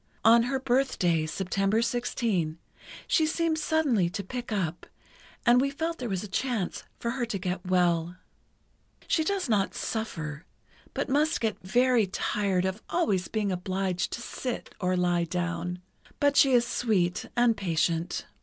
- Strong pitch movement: Yes, wide, 5.7 semitones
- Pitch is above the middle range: Yes, high, 205 Hz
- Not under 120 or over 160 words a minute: Yes, average, 155 wpm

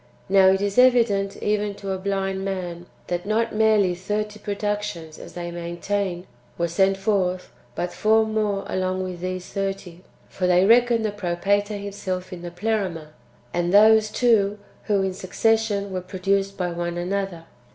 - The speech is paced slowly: No, average, 160 wpm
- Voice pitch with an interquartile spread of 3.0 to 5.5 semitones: No, narrow, 2.4 semitones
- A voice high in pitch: Yes, high, 195 Hz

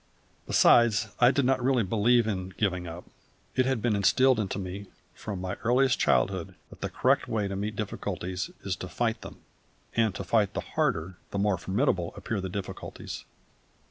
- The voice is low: Yes, low, 105 Hz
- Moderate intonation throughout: Yes, average, 4.1 semitones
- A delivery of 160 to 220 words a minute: Yes, average, 175 wpm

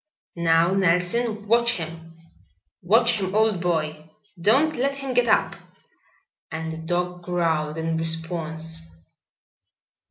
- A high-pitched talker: No, medium, 175 Hz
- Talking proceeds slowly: Yes, slow, 115 wpm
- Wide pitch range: No, average, 5.0 semitones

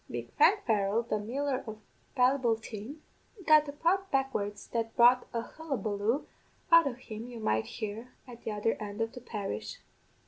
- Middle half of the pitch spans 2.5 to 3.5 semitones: No, average, 4.2 semitones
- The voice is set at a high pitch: Yes, high, 235 Hz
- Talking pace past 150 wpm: Yes, average, 165 wpm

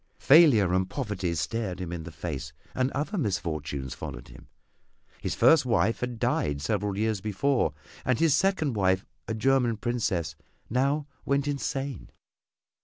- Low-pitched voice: Yes, low, 110 Hz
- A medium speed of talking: Yes, average, 145 wpm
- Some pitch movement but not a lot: No, wide, 6.9 semitones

